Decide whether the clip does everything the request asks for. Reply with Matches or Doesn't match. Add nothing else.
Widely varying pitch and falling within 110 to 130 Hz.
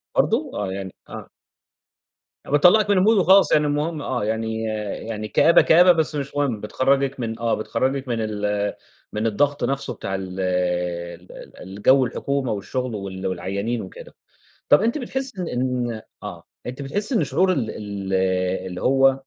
Matches